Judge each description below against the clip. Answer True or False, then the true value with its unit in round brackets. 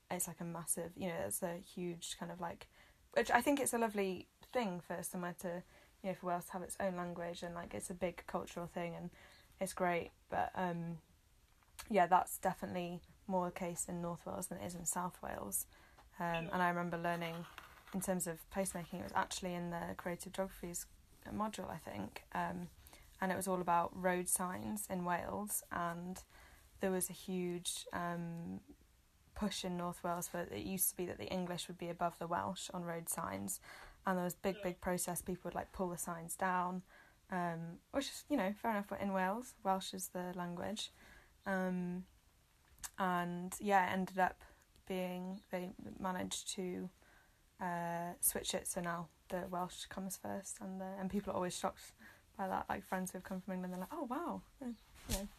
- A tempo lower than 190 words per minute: False (195 wpm)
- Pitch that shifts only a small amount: True (1.6 semitones)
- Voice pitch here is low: False (180 Hz)